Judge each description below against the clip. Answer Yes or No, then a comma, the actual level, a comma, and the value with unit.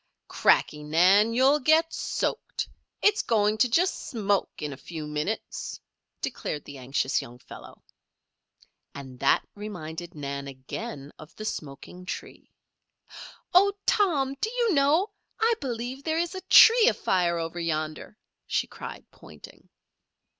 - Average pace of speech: No, slow, 130 wpm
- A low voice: No, high, 205 Hz